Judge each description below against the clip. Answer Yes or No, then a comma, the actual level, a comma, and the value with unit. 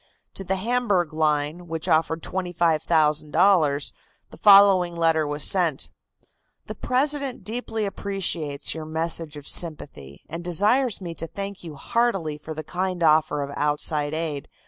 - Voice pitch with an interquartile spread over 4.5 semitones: No, average, 4.1 semitones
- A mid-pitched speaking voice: Yes, medium, 165 Hz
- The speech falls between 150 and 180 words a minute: No, average, 140 wpm